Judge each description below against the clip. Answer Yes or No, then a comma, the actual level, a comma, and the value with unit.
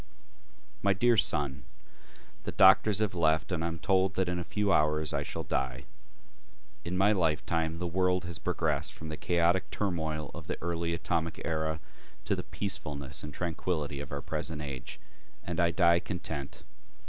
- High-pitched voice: No, very low, 85 Hz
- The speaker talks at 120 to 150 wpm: No, average, 170 wpm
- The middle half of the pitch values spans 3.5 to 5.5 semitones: No, average, 3.0 semitones